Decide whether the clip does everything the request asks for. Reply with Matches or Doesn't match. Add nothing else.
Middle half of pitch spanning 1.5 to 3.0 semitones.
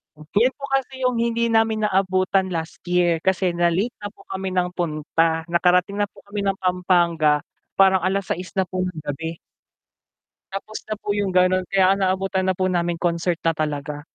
Matches